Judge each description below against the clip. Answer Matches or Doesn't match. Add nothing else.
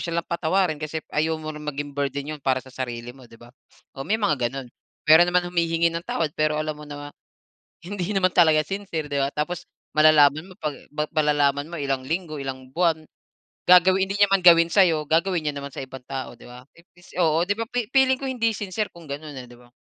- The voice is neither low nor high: Matches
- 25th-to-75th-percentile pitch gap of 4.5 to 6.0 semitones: Doesn't match